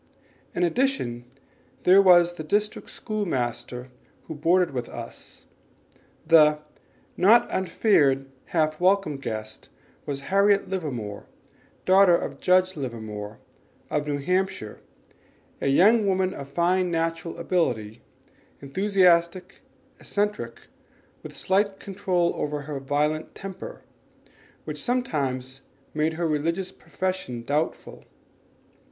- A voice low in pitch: No, medium, 165 Hz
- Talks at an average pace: No, slow, 105 wpm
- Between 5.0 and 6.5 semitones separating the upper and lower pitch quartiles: Yes, wide, 5.4 semitones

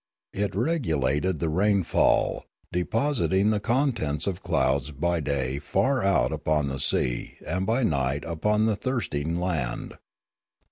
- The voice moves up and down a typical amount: No, wide, 6.7 semitones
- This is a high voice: No, very low, 85 Hz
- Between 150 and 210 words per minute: No, average, 140 wpm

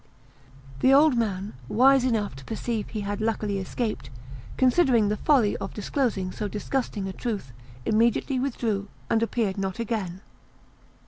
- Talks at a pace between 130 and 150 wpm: Yes, average, 140 wpm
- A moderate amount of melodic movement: Yes, average, 3.5 semitones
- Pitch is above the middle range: Yes, high, 220 Hz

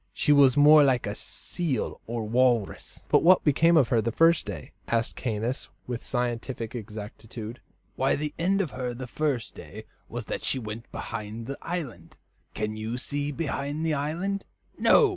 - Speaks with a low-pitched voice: Yes, low, 130 Hz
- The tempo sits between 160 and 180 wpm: Yes, average, 170 wpm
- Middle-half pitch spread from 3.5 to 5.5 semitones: Yes, average, 4.7 semitones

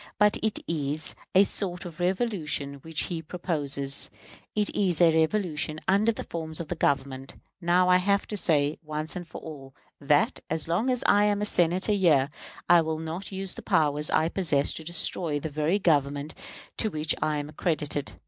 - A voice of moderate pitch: Yes, medium, 160 Hz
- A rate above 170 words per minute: Yes, average, 180 wpm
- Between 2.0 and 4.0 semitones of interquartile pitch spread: Yes, average, 3.7 semitones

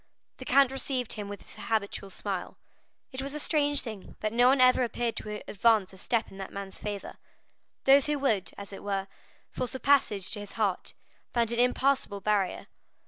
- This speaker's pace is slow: No, average, 195 wpm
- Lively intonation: No, average, 4.5 semitones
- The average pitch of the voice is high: Yes, high, 225 Hz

